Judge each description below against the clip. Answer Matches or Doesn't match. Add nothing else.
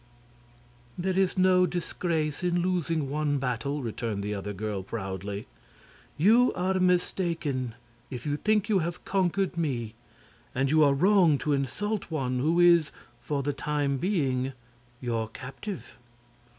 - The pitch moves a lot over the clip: Matches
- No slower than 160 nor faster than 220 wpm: Doesn't match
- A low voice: Doesn't match